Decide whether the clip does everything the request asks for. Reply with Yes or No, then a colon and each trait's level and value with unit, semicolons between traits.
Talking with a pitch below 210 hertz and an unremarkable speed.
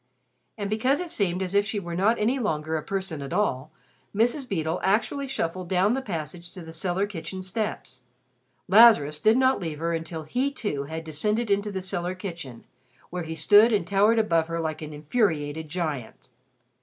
Yes: medium, 185 Hz; average, 185 wpm